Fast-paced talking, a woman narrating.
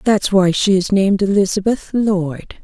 No: average, 160 wpm; female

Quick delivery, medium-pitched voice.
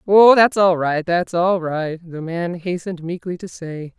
No: average, 195 wpm; medium, 175 Hz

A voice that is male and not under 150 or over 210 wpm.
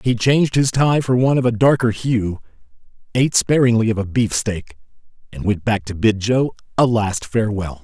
Yes: male; average, 185 wpm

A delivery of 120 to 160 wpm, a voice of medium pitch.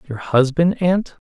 Yes: average, 140 wpm; medium, 155 Hz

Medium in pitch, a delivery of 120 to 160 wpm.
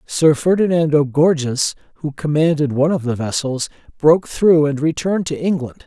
Yes: medium, 150 Hz; average, 155 wpm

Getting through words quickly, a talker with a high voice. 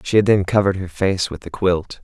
No: fast, 265 wpm; very low, 90 Hz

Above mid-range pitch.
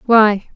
Yes: high, 215 Hz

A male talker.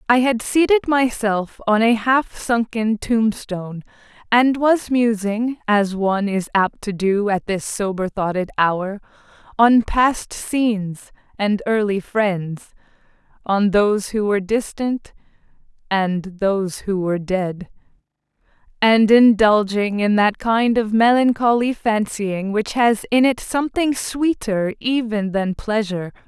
No: female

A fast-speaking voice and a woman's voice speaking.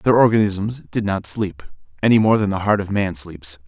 No: fast, 210 wpm; male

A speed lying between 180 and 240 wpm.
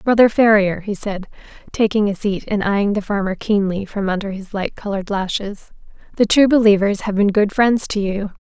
Yes: average, 190 wpm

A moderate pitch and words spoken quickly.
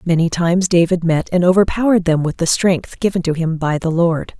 Yes: medium, 175 Hz; fast, 220 wpm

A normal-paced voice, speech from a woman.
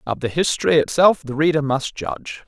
No: average, 195 wpm; male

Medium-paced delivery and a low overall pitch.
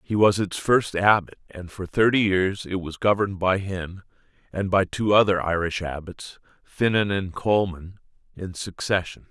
Yes: average, 160 wpm; very low, 95 Hz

